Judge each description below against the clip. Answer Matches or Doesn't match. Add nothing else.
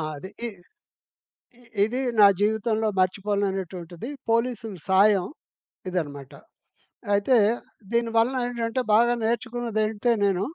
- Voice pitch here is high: Matches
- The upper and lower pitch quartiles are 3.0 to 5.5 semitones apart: Matches